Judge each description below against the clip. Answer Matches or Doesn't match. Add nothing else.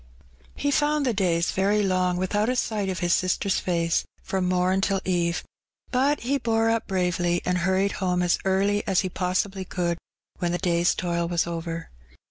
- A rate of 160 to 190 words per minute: Matches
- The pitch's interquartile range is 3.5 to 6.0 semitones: Doesn't match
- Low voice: Doesn't match